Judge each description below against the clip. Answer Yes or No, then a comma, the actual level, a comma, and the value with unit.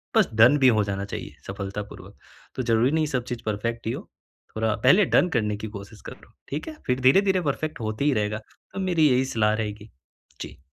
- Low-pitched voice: Yes, low, 115 Hz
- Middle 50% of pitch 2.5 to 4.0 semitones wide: No, average, 5.1 semitones